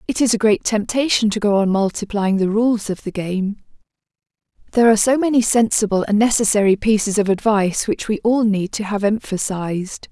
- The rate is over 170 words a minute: Yes, average, 185 wpm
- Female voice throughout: Yes, female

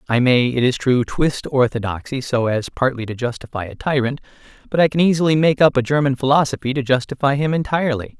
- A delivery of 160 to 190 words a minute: No, average, 200 wpm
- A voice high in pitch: No, low, 130 Hz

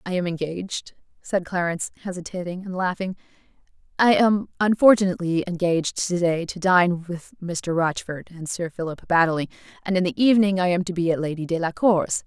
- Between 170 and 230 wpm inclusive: No, average, 160 wpm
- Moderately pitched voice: Yes, medium, 175 Hz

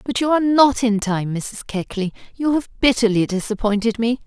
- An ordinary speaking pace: Yes, average, 185 wpm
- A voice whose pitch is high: Yes, high, 230 Hz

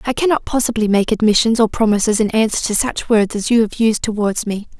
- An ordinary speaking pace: No, fast, 225 wpm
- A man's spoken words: No, female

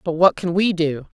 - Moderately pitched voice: Yes, medium, 170 Hz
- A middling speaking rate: No, fast, 250 wpm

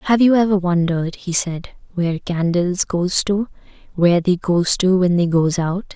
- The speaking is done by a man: No, female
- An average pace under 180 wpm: Yes, average, 170 wpm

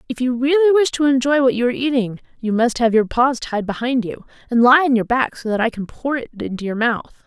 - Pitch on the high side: Yes, very high, 250 Hz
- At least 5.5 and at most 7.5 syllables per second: Yes, 5.8 syllables/s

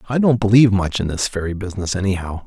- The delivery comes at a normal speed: No, fast, 220 wpm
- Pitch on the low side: Yes, low, 100 Hz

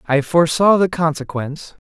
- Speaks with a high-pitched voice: No, medium, 160 Hz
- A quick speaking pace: No, slow, 130 wpm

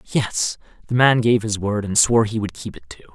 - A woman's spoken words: No, male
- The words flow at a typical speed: No, fast, 250 wpm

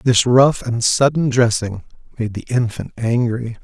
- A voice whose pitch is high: No, low, 120 Hz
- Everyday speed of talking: Yes, average, 150 wpm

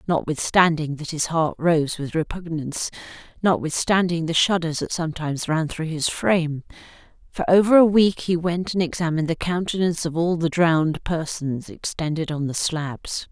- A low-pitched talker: No, medium, 165 Hz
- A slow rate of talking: No, average, 160 wpm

